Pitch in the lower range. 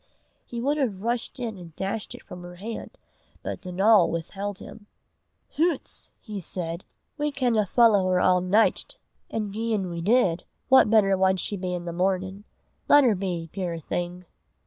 No: high, 195 Hz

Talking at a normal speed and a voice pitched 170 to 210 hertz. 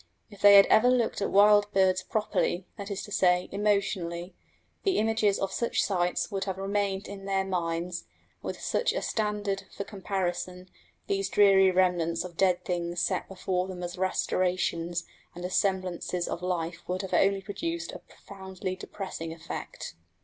Yes: average, 165 wpm; high, 190 Hz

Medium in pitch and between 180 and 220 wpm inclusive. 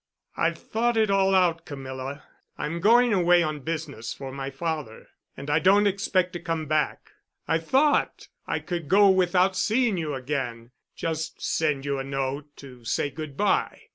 No: medium, 160 Hz; average, 165 wpm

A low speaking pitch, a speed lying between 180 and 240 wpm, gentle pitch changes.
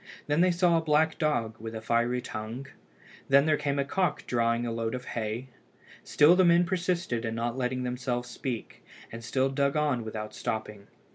No: low, 125 Hz; average, 190 wpm; average, 4.7 semitones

